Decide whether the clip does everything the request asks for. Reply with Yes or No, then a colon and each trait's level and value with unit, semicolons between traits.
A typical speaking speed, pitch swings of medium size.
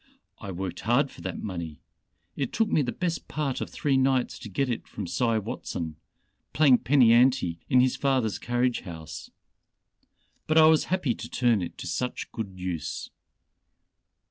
No: average, 170 wpm; wide, 5.9 semitones